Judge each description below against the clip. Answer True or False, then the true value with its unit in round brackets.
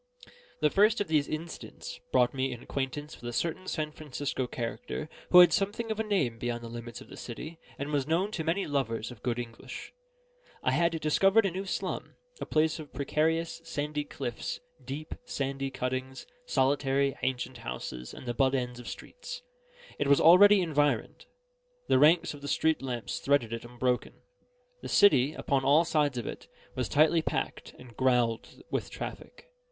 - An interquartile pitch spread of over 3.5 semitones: True (4.5 semitones)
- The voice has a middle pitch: True (145 Hz)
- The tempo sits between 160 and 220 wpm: True (175 wpm)